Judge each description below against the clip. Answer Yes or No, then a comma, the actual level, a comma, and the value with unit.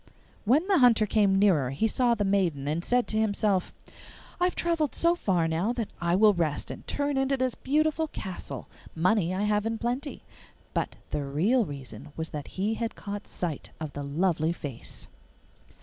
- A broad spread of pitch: Yes, wide, 6.9 semitones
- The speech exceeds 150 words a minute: Yes, average, 180 wpm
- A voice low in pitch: No, high, 205 Hz